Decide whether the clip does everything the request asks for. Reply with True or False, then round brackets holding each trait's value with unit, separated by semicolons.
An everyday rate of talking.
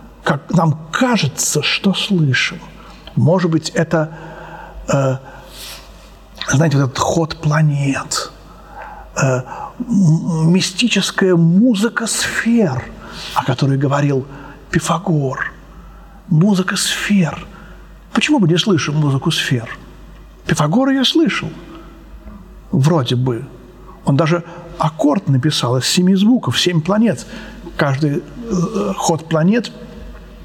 False (95 wpm)